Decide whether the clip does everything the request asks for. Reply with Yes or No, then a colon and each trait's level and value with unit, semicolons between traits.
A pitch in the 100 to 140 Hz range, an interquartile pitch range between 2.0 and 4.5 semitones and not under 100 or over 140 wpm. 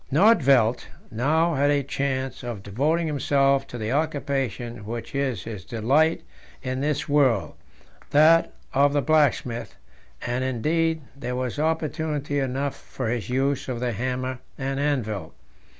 Yes: low, 135 Hz; average, 3.2 semitones; slow, 135 wpm